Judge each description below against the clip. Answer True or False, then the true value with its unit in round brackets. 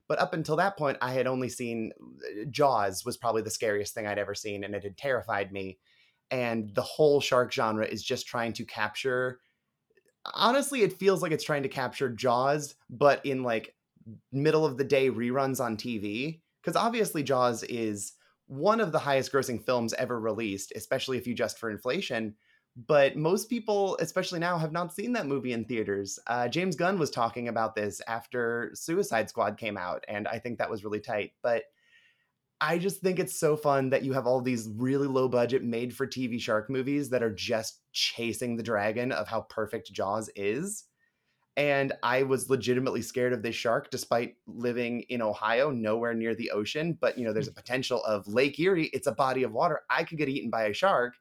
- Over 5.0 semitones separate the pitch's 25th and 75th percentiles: False (4.3 semitones)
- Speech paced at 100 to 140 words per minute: False (200 wpm)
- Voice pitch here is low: True (125 Hz)